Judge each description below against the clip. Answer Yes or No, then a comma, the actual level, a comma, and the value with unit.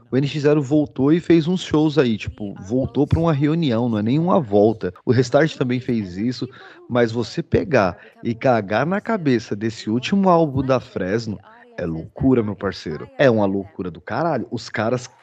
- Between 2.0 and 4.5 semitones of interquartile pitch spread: No, wide, 5.5 semitones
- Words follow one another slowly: No, average, 175 wpm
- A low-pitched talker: Yes, low, 125 Hz